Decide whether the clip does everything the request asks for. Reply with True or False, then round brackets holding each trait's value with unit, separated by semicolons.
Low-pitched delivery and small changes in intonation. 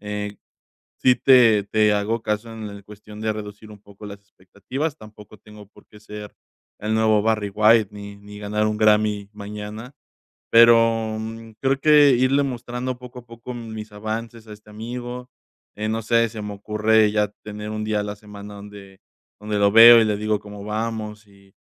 True (105 Hz; 1.7 semitones)